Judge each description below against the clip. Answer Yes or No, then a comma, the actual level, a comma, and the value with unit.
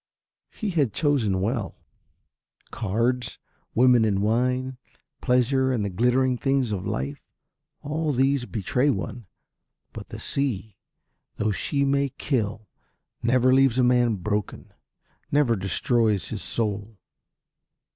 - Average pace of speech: No, slow, 115 wpm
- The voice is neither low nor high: No, low, 120 Hz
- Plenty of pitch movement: No, average, 3.9 semitones